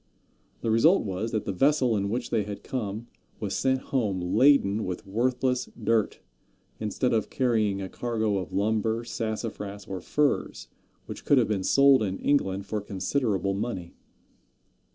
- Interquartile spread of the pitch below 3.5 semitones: No, average, 3.9 semitones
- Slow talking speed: No, average, 155 wpm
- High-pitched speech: No, low, 110 Hz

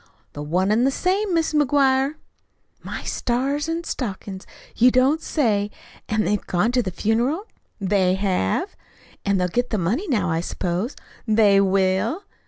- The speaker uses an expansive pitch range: Yes, wide, 6.2 semitones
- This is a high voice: Yes, high, 220 Hz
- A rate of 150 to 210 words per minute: Yes, average, 155 wpm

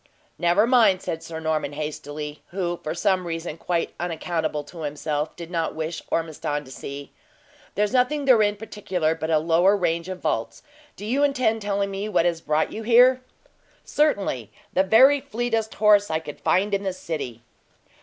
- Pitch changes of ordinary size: Yes, average, 4.9 semitones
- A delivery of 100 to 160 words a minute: No, average, 170 wpm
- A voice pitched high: No, medium, 175 Hz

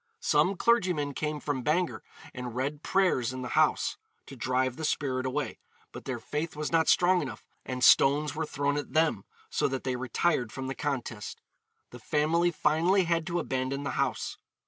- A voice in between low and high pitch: Yes, medium, 145 Hz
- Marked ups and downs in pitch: No, average, 3.9 semitones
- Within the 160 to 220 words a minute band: Yes, average, 180 wpm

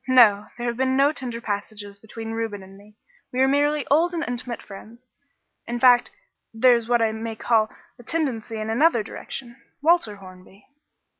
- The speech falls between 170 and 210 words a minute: Yes, average, 175 wpm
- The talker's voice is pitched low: No, high, 235 Hz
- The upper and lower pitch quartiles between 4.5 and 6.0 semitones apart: No, average, 3.3 semitones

